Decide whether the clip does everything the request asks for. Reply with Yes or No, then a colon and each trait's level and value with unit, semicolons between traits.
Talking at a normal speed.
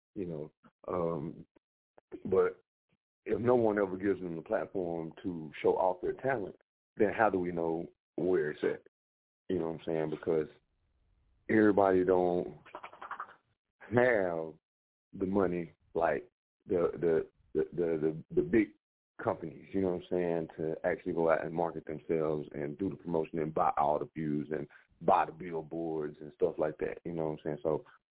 Yes: average, 170 wpm